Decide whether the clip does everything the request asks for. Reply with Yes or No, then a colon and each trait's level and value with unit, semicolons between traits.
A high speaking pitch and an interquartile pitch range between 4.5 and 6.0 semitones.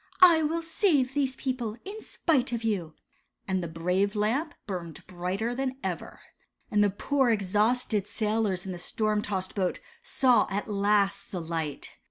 Yes: high, 210 Hz; wide, 5.4 semitones